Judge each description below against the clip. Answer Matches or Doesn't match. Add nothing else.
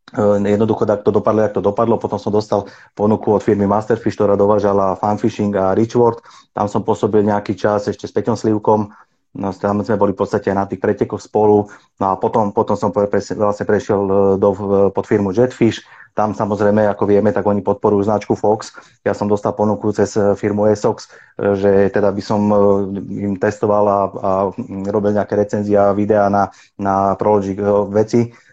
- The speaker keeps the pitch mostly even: Matches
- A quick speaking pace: Matches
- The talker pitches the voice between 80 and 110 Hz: Matches